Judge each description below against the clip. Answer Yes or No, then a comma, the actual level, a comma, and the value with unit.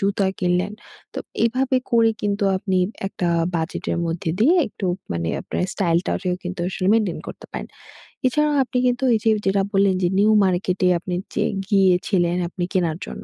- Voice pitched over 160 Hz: Yes, high, 190 Hz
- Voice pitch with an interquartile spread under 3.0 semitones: No, average, 3.5 semitones